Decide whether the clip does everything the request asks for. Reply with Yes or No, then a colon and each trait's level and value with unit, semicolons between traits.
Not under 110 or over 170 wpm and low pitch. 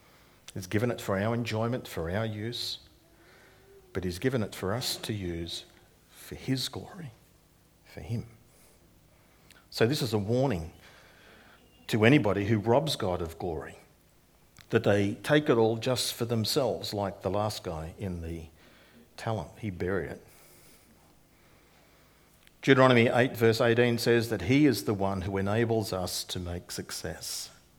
Yes: average, 145 wpm; low, 110 Hz